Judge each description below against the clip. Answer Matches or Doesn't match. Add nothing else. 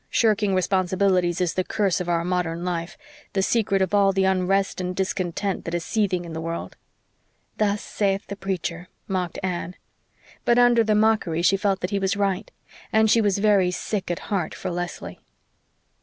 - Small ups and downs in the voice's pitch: Matches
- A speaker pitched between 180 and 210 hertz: Matches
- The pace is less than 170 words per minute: Doesn't match